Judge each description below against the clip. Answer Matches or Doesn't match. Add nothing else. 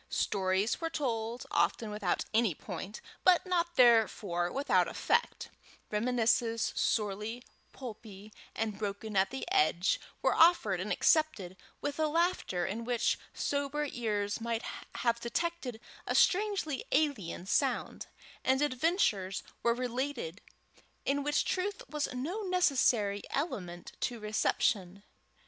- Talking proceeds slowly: Matches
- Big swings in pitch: Matches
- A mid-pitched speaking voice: Doesn't match